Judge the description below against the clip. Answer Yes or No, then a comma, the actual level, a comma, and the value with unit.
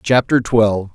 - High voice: No, low, 110 Hz